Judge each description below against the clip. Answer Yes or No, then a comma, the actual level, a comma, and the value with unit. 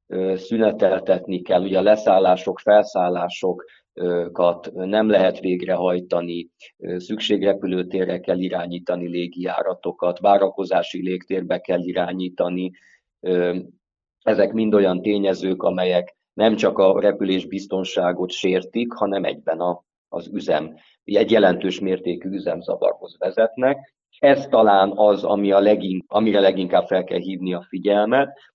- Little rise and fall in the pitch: Yes, narrow, 2.3 semitones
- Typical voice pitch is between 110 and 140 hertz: No, very low, 95 Hz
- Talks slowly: Yes, slow, 100 wpm